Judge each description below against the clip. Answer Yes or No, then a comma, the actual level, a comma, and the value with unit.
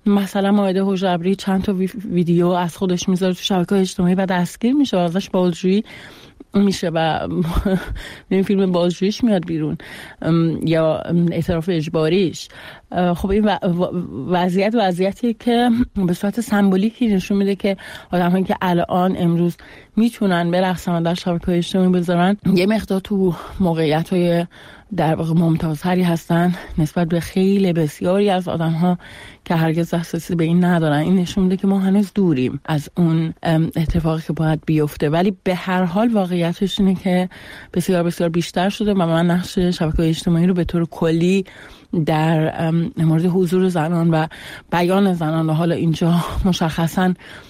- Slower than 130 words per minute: No, average, 150 wpm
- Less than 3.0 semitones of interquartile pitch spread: Yes, narrow, 2.4 semitones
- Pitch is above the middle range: No, medium, 180 Hz